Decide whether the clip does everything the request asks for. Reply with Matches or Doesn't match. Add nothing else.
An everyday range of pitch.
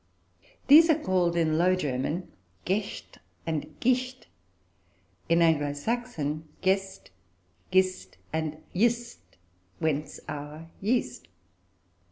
Doesn't match